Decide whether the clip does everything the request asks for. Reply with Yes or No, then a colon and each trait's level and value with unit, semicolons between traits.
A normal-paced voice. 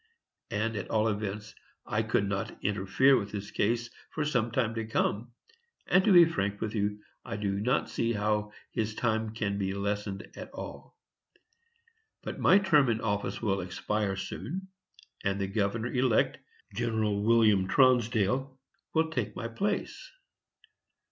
Yes: average, 150 wpm